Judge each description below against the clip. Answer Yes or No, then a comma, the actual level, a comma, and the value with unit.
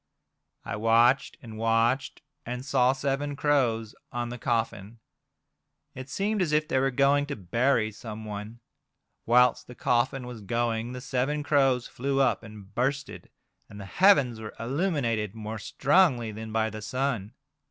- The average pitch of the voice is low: Yes, low, 120 Hz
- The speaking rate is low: No, average, 150 wpm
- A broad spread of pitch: No, average, 3.6 semitones